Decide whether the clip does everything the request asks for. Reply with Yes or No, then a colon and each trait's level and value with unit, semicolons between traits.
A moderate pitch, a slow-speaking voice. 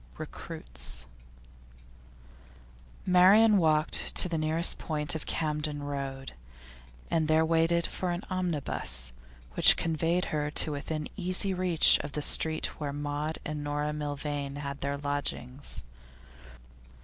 Yes: medium, 150 Hz; slow, 120 wpm